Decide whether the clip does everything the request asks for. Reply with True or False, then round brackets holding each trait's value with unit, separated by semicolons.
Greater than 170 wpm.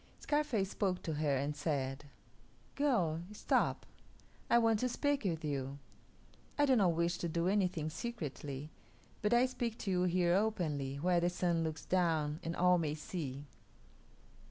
False (155 wpm)